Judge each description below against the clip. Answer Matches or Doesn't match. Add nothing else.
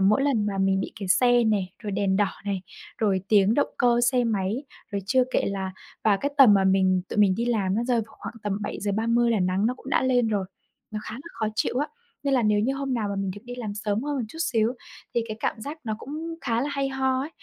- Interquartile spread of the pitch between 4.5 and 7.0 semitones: Doesn't match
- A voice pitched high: Matches